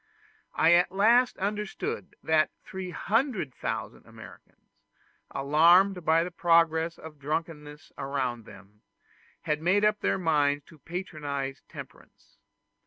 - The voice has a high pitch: No, medium, 165 Hz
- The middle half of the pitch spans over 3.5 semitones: Yes, average, 4.1 semitones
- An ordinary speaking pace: No, slow, 105 wpm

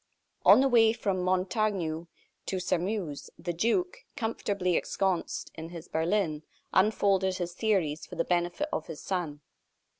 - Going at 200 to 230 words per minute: No, average, 140 wpm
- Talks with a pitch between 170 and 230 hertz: Yes, medium, 185 Hz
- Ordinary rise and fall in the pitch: Yes, average, 3.8 semitones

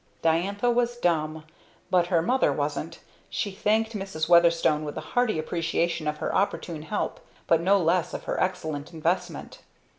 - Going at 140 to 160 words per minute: Yes, average, 155 wpm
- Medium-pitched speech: Yes, medium, 170 Hz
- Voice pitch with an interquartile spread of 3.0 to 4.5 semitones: Yes, average, 4.0 semitones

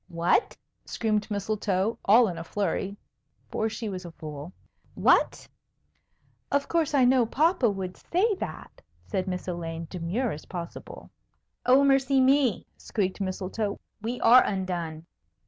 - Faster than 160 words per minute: No, slow, 135 wpm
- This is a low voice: No, high, 205 Hz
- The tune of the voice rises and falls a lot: Yes, wide, 5.7 semitones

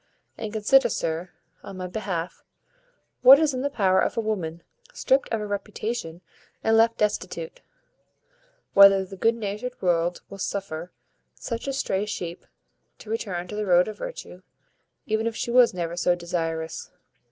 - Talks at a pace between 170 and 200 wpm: No, average, 160 wpm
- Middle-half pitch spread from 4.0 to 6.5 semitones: Yes, average, 4.5 semitones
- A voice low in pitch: No, high, 205 Hz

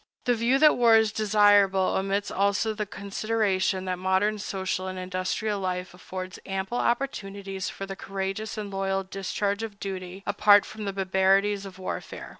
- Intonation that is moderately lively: No, narrow, 1.8 semitones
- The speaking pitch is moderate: No, high, 195 Hz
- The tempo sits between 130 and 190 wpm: Yes, average, 160 wpm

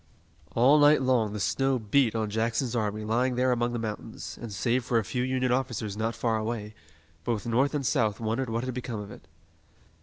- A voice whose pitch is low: Yes, low, 115 Hz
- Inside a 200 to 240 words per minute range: Yes, fast, 205 wpm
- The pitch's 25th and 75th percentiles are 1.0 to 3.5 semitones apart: Yes, average, 2.8 semitones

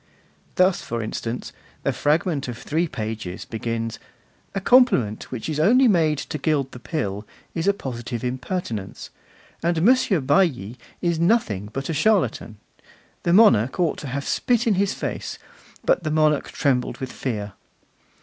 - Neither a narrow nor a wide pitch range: No, wide, 7.2 semitones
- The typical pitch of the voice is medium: Yes, medium, 145 Hz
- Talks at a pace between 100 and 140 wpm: No, average, 150 wpm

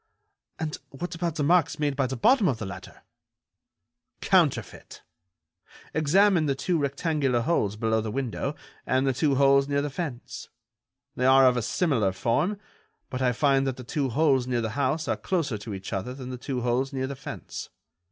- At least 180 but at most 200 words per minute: Yes, average, 185 wpm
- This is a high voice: No, low, 135 Hz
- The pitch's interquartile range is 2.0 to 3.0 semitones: No, average, 3.5 semitones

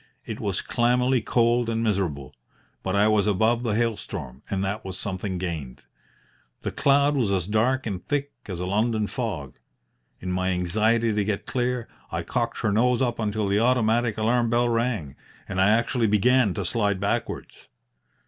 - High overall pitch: No, low, 110 Hz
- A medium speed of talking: Yes, average, 175 wpm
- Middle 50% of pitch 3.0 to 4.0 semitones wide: Yes, average, 3.6 semitones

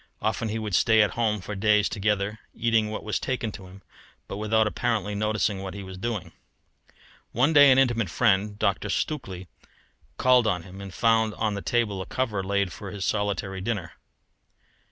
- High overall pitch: No, low, 105 Hz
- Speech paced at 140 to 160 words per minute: No, average, 180 wpm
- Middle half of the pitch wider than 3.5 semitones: No, average, 2.7 semitones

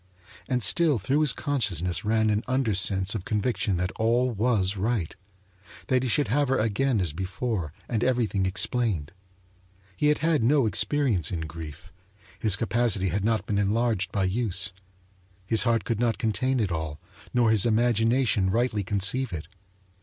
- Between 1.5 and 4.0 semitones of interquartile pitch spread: No, average, 4.5 semitones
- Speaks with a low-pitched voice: Yes, low, 110 Hz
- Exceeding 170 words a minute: No, average, 160 wpm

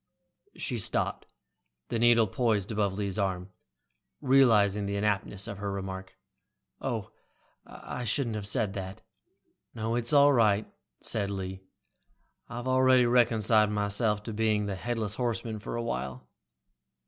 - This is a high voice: No, low, 105 Hz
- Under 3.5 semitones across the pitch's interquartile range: Yes, average, 3.0 semitones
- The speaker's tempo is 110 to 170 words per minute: Yes, slow, 135 wpm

